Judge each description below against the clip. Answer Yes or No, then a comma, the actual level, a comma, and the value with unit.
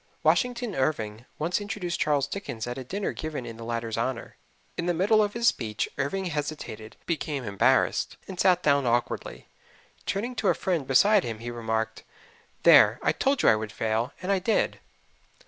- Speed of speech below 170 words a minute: No, average, 180 wpm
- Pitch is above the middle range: No, medium, 145 Hz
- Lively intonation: Yes, wide, 8.7 semitones